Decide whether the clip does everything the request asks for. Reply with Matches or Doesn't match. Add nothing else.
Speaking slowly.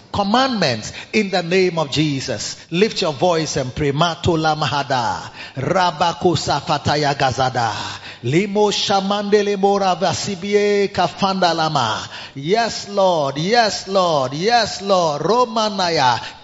Matches